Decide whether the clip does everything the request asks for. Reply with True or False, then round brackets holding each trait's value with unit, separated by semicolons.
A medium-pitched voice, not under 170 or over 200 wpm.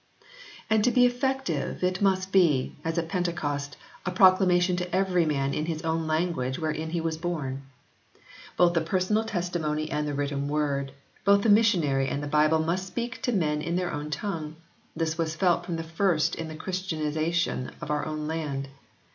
True (165 Hz; 180 wpm)